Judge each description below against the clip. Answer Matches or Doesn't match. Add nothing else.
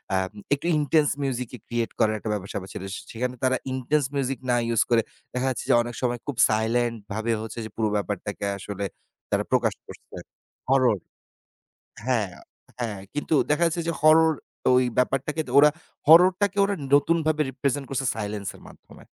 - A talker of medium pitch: Doesn't match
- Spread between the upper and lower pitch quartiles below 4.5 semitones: Doesn't match